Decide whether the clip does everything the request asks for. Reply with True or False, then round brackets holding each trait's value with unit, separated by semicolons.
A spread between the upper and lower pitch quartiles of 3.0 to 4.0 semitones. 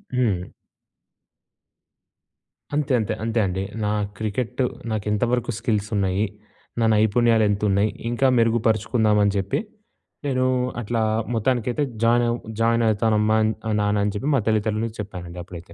False (2.5 semitones)